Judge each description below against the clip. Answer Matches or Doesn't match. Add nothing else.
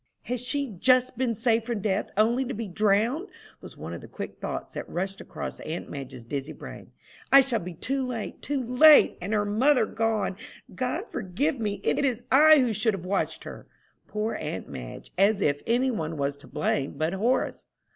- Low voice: Doesn't match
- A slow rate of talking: Doesn't match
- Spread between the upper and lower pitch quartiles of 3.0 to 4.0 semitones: Doesn't match